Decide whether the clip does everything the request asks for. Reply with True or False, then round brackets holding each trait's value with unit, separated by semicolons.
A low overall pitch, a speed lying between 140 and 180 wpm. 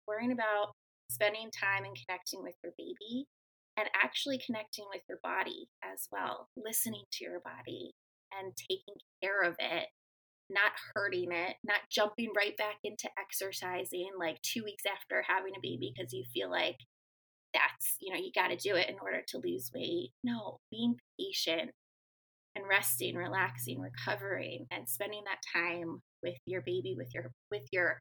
False (195 Hz; 165 wpm)